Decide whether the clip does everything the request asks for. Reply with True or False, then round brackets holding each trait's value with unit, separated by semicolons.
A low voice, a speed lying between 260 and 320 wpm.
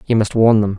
True (105 Hz; 305 wpm)